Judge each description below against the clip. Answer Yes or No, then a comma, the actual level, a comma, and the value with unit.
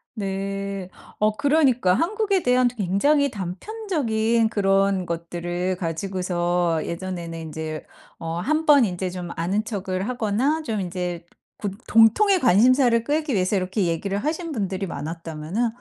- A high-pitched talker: Yes, high, 195 Hz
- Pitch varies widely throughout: Yes, wide, 5.8 semitones